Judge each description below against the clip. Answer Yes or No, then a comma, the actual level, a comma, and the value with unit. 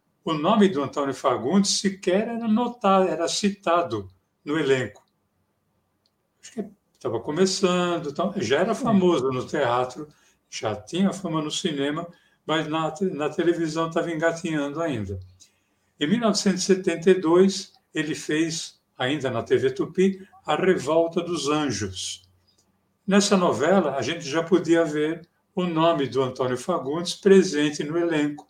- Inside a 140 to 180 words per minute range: No, average, 125 wpm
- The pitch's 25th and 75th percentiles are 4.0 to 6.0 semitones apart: Yes, average, 4.5 semitones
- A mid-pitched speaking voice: Yes, medium, 165 Hz